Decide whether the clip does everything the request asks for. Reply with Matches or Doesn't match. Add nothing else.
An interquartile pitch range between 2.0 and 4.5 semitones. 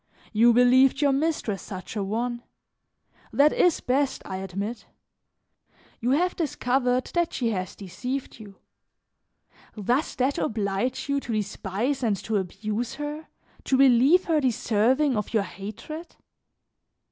Doesn't match